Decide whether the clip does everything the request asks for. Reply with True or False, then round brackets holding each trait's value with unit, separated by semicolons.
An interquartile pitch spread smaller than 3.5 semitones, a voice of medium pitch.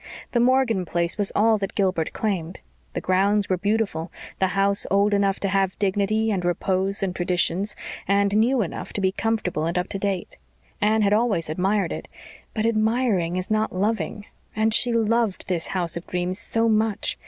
False (2.8 semitones; 200 Hz)